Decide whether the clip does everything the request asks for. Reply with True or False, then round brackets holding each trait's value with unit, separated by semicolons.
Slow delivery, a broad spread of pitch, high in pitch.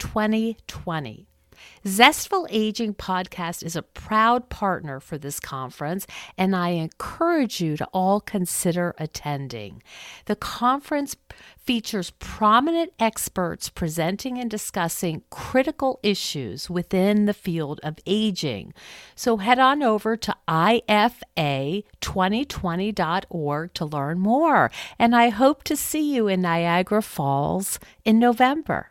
True (115 wpm; 5.7 semitones; 195 Hz)